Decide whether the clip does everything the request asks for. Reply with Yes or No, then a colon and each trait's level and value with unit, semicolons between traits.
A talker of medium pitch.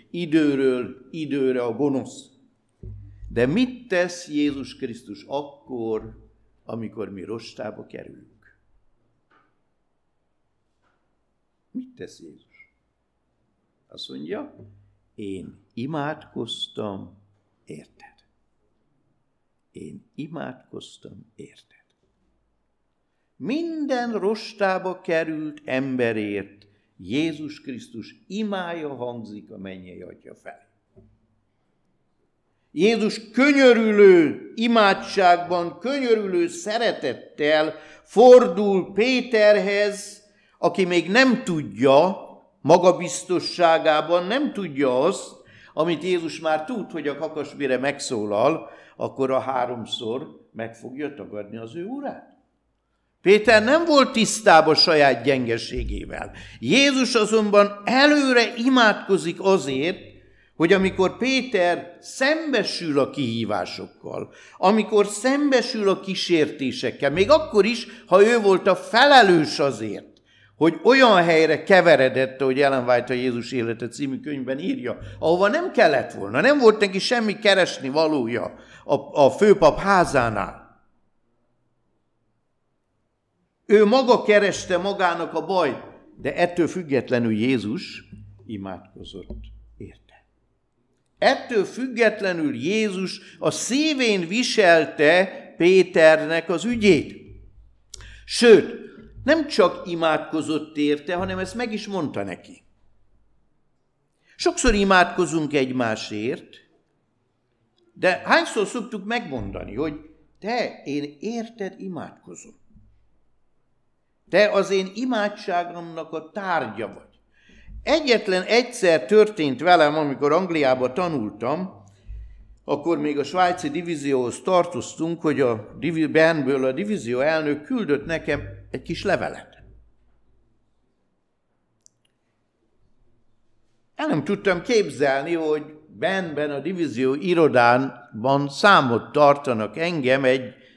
Yes: medium, 160 Hz